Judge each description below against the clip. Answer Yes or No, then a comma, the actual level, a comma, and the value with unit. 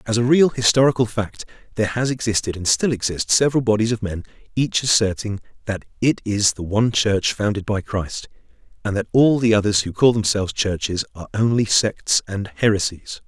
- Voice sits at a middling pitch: No, low, 110 Hz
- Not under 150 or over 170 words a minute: No, average, 180 wpm